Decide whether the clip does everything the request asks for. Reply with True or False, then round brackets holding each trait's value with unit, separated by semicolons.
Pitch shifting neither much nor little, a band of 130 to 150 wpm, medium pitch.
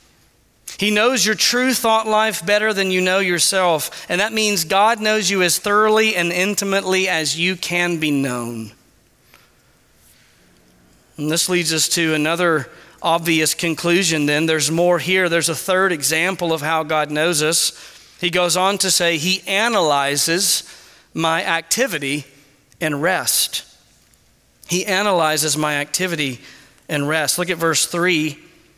True (3.5 semitones; 140 wpm; 170 Hz)